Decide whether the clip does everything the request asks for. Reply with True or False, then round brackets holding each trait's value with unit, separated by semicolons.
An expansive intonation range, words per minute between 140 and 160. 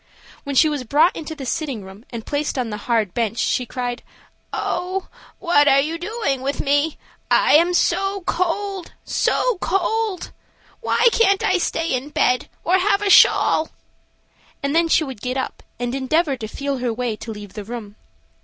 False (6.1 semitones; 175 wpm)